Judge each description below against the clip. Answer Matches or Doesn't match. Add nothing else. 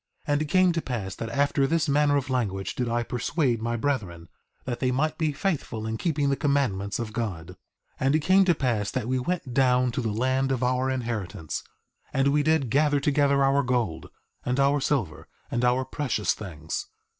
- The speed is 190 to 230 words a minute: Matches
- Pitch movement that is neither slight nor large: Matches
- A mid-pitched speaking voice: Doesn't match